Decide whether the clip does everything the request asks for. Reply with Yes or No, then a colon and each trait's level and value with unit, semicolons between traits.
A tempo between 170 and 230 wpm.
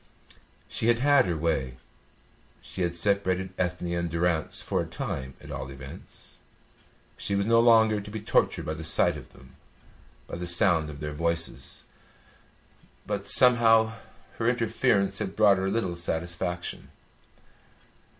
No: average, 145 wpm